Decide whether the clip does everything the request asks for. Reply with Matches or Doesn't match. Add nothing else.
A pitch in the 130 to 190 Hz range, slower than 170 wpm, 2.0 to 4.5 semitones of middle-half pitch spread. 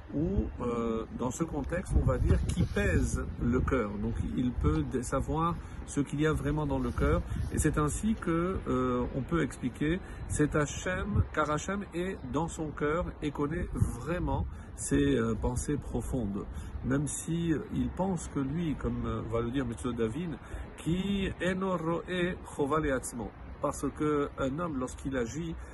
Doesn't match